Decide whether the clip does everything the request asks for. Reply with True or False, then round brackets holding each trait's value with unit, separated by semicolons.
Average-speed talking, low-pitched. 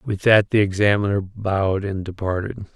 True (155 wpm; 100 Hz)